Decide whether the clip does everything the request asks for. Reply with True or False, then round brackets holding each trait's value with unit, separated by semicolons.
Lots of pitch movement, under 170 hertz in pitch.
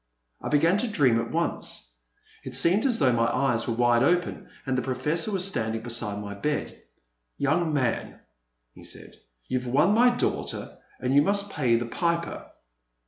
True (6.7 semitones; 140 Hz)